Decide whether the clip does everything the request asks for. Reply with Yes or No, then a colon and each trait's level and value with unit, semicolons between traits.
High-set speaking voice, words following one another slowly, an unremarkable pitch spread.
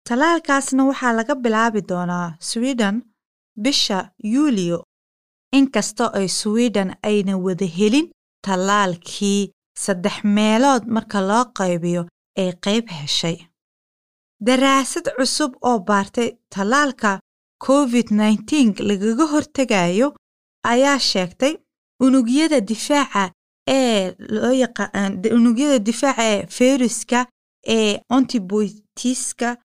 Yes: high, 225 Hz; slow, 90 wpm; average, 4.7 semitones